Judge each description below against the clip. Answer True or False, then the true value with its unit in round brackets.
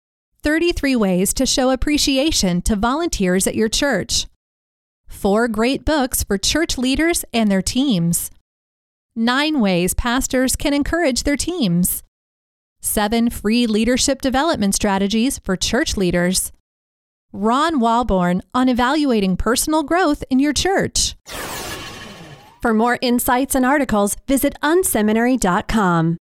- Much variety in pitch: True (6.7 semitones)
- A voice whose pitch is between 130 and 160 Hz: False (235 Hz)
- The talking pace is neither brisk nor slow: False (115 wpm)